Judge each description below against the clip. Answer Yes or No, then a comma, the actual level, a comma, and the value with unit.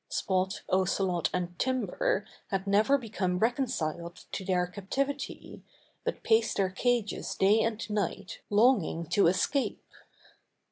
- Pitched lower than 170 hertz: No, high, 200 Hz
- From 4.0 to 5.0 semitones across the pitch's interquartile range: Yes, average, 4.5 semitones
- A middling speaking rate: No, slow, 120 wpm